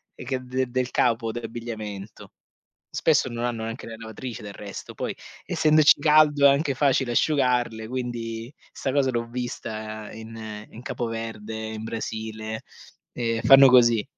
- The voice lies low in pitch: Yes, low, 115 Hz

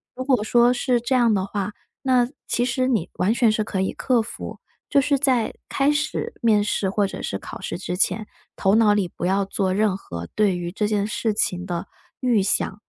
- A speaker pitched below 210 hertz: No, high, 215 Hz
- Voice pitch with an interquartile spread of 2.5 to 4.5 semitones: Yes, average, 4.1 semitones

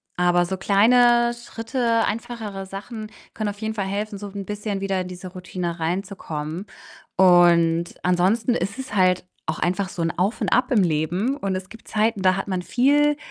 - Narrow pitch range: No, average, 3.6 semitones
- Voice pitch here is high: Yes, high, 195 Hz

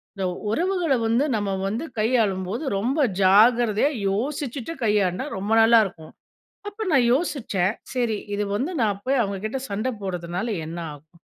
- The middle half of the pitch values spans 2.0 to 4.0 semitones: No, average, 4.9 semitones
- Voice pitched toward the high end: Yes, high, 220 Hz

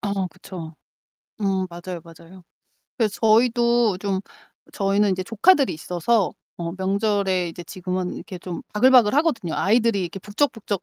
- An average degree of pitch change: Yes, average, 3.6 semitones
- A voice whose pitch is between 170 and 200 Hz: Yes, high, 195 Hz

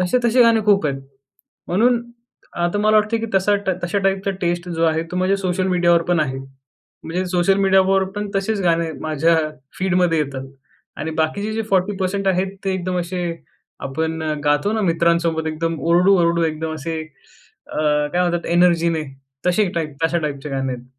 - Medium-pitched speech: Yes, medium, 175 Hz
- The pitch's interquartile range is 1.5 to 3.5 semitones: Yes, average, 3.2 semitones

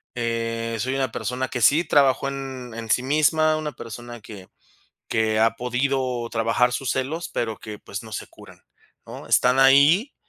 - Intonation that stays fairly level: No, average, 3.0 semitones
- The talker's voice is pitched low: Yes, low, 125 Hz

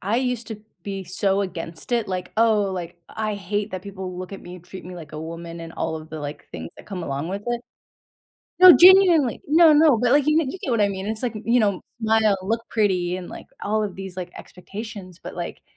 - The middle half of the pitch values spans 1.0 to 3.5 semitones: No, average, 4.2 semitones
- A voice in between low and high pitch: No, high, 200 Hz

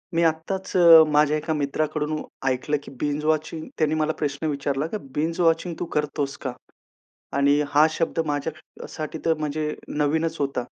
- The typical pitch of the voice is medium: Yes, medium, 155 Hz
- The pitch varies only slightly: Yes, narrow, 1.7 semitones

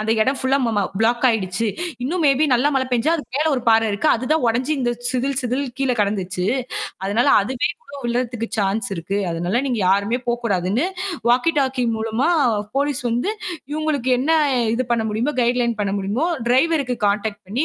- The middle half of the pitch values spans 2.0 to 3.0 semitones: No, average, 3.7 semitones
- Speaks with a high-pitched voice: Yes, high, 240 Hz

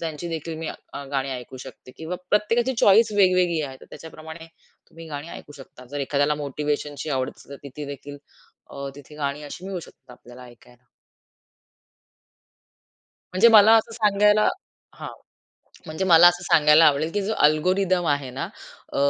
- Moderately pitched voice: Yes, medium, 155 Hz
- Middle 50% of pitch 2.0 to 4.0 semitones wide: No, average, 4.4 semitones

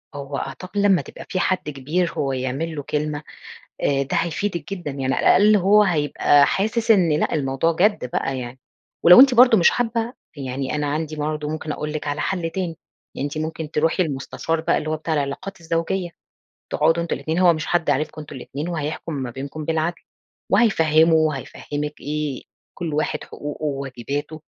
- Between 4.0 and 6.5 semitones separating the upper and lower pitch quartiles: No, average, 3.2 semitones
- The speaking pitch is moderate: Yes, medium, 155 Hz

